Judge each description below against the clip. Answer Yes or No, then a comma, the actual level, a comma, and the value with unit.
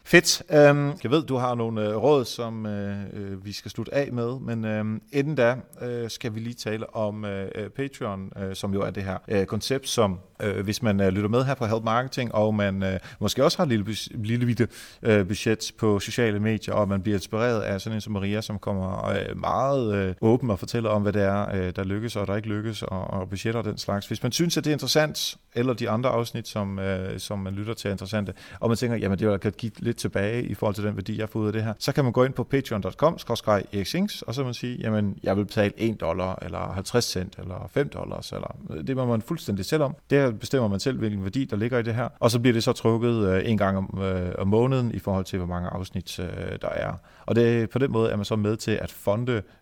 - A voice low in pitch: Yes, low, 110 Hz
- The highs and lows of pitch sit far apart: No, average, 3.3 semitones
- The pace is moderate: No, fast, 245 wpm